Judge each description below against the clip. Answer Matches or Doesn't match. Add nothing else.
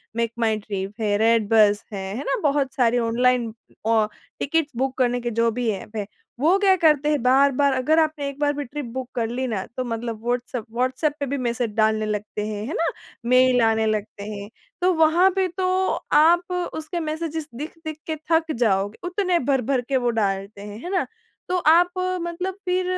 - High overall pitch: Matches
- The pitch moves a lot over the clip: Matches